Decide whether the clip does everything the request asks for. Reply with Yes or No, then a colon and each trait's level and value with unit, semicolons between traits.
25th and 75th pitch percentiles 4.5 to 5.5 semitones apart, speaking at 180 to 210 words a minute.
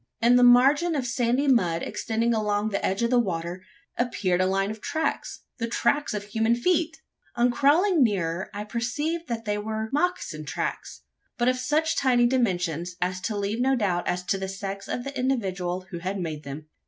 Yes: average, 5.2 semitones; average, 190 wpm